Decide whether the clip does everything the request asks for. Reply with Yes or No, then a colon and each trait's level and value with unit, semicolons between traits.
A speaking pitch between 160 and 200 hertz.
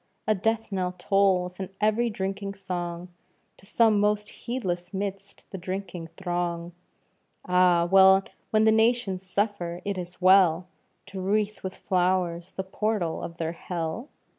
Yes: high, 190 Hz